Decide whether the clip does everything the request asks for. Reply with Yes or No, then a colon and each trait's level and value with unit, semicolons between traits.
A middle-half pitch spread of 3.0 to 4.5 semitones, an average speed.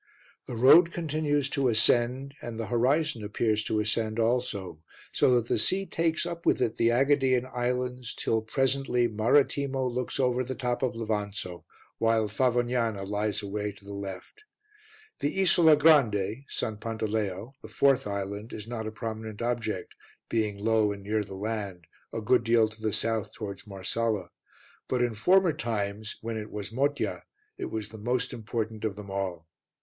Yes: average, 3.3 semitones; average, 165 wpm